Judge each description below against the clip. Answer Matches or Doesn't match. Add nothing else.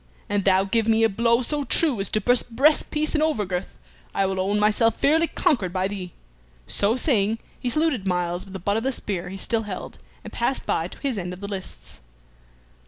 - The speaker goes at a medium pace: Doesn't match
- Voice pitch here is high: Matches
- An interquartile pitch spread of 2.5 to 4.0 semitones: Doesn't match